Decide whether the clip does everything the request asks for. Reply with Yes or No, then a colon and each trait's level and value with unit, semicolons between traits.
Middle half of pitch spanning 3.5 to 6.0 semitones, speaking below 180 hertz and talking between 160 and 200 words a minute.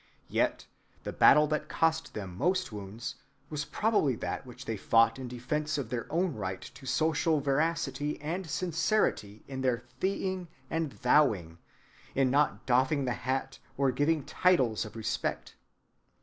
No: average, 5.2 semitones; low, 135 Hz; average, 150 wpm